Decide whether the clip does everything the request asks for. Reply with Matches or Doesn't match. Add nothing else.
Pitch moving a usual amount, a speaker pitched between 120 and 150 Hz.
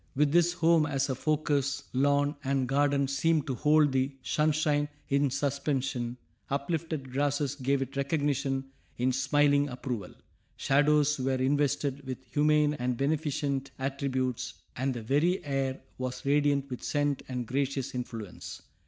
Doesn't match